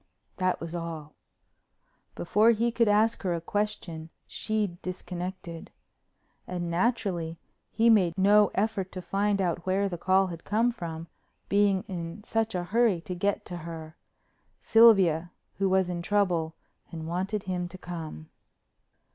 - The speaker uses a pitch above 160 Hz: Yes, medium, 185 Hz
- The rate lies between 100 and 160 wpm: Yes, average, 140 wpm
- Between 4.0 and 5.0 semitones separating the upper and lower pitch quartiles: No, average, 3.4 semitones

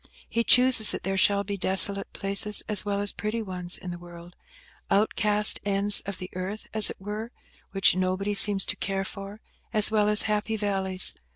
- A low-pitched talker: No, high, 200 Hz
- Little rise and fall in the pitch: Yes, narrow, 1.7 semitones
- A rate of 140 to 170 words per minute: No, average, 185 wpm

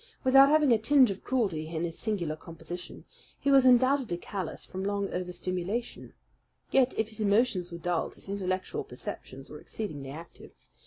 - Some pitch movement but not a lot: No, wide, 6.1 semitones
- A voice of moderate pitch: No, high, 200 Hz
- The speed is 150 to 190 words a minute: Yes, average, 160 wpm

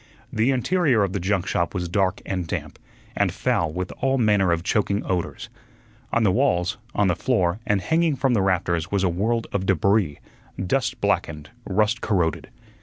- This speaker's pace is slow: No, average, 180 wpm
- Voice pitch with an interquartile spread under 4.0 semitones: No, average, 4.4 semitones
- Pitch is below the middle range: Yes, low, 100 Hz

